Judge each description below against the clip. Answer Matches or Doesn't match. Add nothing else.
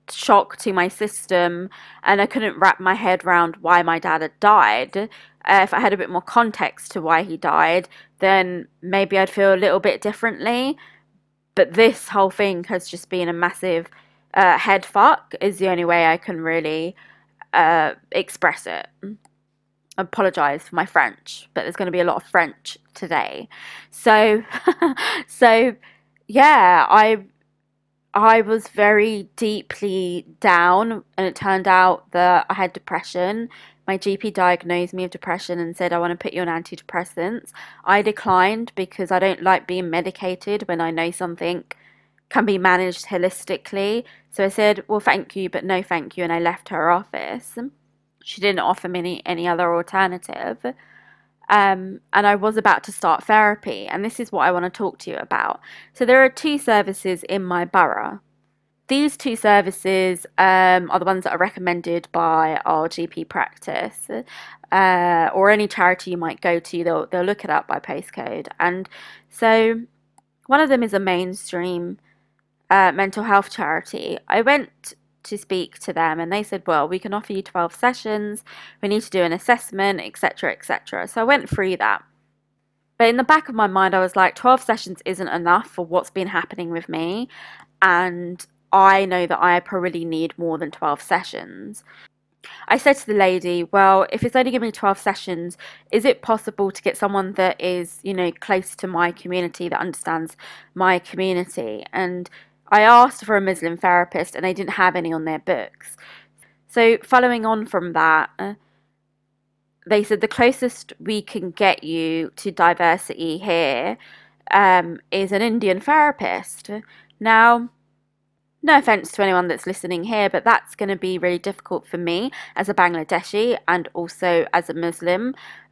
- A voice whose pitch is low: Doesn't match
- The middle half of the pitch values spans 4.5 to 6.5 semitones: Doesn't match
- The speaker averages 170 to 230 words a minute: Matches